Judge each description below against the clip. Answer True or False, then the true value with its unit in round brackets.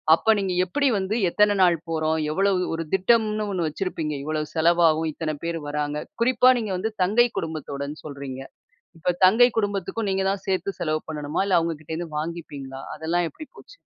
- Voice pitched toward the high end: False (170 Hz)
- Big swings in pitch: False (4.3 semitones)